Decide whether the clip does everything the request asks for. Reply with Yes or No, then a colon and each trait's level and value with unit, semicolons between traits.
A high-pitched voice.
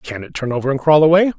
No: medium, 145 Hz